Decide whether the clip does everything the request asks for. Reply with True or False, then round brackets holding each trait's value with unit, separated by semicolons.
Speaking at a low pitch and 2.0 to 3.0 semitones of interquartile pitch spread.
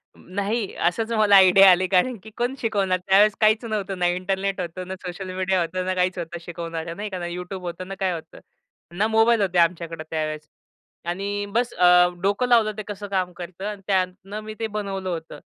False (190 Hz; 2.5 semitones)